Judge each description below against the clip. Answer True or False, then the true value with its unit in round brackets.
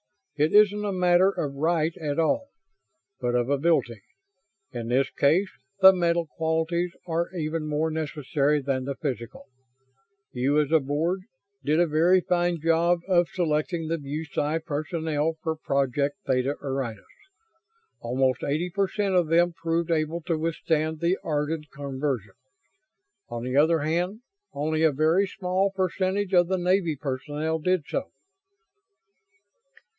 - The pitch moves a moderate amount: True (3.3 semitones)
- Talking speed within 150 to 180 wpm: False (140 wpm)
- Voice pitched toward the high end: False (160 Hz)